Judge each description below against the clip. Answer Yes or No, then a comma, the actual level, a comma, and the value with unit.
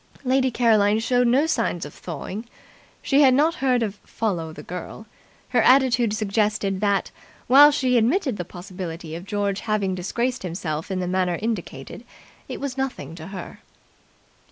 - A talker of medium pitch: No, high, 210 Hz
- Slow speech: No, average, 155 wpm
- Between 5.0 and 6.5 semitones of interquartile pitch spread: Yes, wide, 5.6 semitones